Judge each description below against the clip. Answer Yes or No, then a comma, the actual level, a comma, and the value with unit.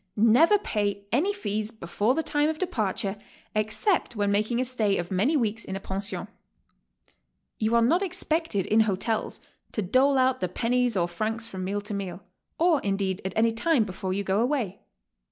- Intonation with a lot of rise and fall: No, average, 4.6 semitones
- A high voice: Yes, high, 220 Hz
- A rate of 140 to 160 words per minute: No, average, 185 wpm